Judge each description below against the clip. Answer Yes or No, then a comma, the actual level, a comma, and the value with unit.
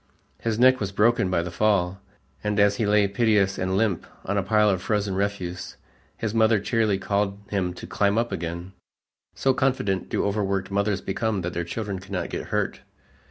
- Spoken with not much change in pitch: Yes, narrow, 2.3 semitones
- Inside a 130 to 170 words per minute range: No, average, 185 wpm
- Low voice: Yes, low, 100 Hz